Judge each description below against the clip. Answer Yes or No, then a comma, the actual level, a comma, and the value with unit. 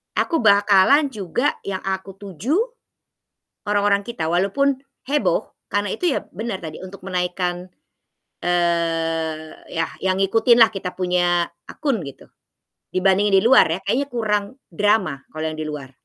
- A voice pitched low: No, high, 190 Hz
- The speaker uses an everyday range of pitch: Yes, average, 3.3 semitones